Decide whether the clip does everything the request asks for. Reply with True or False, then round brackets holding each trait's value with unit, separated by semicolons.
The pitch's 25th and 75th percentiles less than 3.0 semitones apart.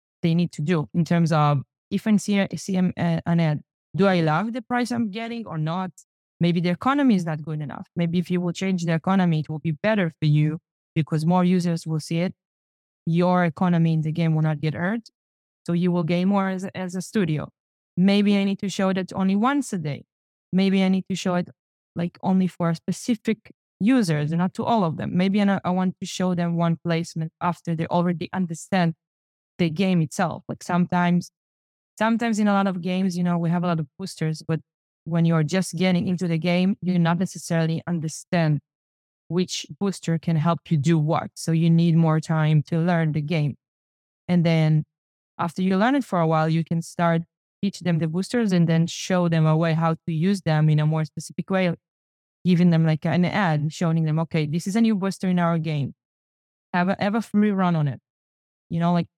True (2.6 semitones)